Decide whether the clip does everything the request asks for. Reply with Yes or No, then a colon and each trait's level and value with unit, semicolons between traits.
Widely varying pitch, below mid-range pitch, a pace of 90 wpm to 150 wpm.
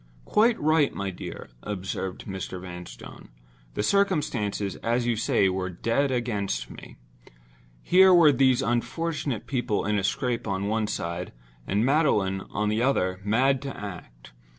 Yes: wide, 6.0 semitones; low, 110 Hz; average, 145 wpm